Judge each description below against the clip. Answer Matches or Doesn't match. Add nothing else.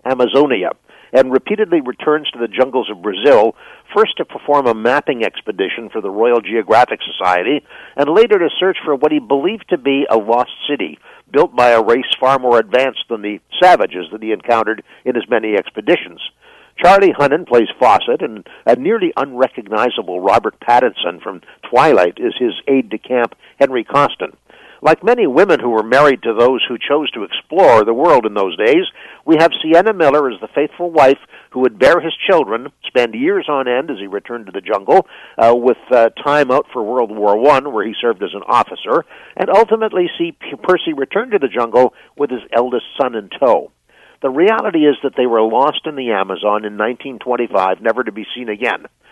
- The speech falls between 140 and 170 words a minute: Doesn't match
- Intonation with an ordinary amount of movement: Doesn't match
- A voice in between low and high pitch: Matches